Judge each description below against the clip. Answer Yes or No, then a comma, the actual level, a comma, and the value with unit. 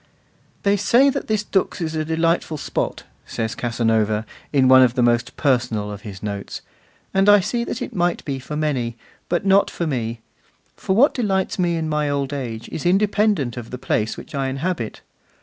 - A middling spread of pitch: No, wide, 8.0 semitones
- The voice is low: No, medium, 145 Hz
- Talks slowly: No, average, 190 wpm